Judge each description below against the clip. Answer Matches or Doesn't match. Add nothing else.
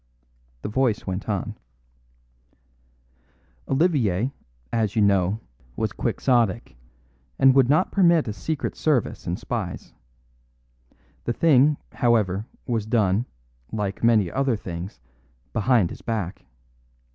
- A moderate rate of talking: Doesn't match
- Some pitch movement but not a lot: Matches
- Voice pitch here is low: Matches